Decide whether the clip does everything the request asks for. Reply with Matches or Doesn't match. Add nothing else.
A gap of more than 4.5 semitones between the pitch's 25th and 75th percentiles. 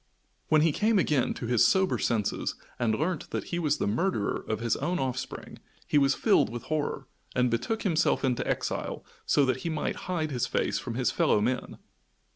Matches